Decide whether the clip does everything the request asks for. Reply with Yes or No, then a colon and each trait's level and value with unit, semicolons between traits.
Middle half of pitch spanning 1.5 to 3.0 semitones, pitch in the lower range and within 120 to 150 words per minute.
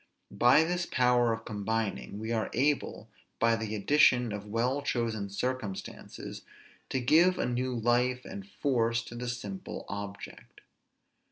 Yes: narrow, 2.6 semitones; low, 120 Hz; average, 140 wpm